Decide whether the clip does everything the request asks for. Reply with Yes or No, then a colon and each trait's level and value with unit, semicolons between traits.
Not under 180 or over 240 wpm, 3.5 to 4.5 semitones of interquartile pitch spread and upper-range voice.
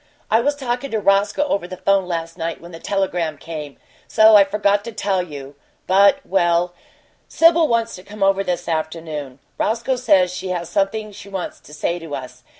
Yes: average, 190 wpm; average, 4.0 semitones; high, 195 Hz